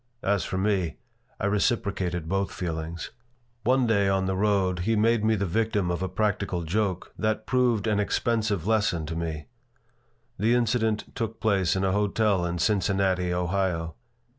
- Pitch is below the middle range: Yes, low, 100 Hz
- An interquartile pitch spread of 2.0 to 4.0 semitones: Yes, average, 3.4 semitones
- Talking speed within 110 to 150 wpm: No, average, 160 wpm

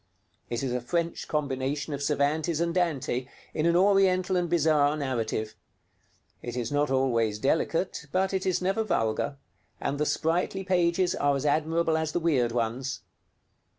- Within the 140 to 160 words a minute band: Yes, average, 155 wpm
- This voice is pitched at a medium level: Yes, medium, 150 Hz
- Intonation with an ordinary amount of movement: Yes, average, 4.7 semitones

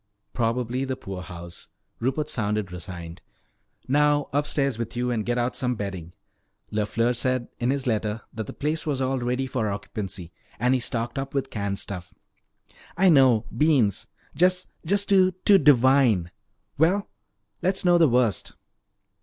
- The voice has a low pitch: Yes, low, 125 Hz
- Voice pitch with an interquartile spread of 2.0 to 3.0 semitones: No, average, 4.8 semitones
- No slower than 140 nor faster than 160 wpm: Yes, average, 145 wpm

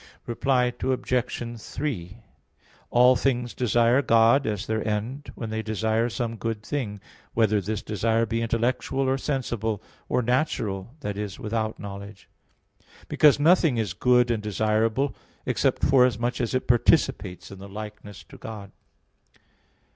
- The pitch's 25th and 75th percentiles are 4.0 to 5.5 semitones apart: No, average, 2.9 semitones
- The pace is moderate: No, slow, 130 wpm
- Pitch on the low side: Yes, low, 115 Hz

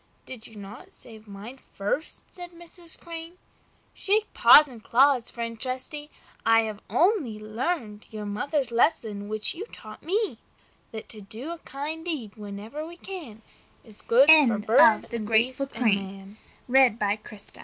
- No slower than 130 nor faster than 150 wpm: Yes, average, 145 wpm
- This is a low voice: No, high, 235 Hz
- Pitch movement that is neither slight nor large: No, wide, 6.3 semitones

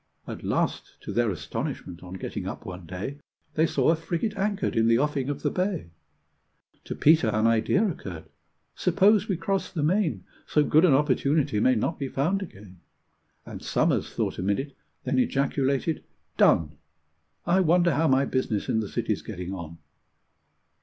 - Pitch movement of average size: No, wide, 7.9 semitones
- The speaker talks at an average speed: Yes, average, 165 wpm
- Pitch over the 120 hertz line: Yes, medium, 140 Hz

